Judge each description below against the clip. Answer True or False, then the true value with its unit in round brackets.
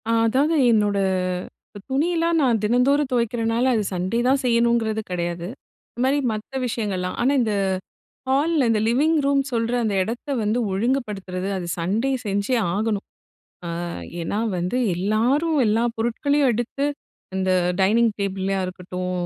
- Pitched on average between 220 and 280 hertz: True (225 Hz)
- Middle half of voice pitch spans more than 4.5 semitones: True (5.0 semitones)